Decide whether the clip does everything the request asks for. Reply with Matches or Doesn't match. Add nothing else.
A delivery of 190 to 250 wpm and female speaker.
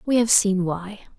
Matches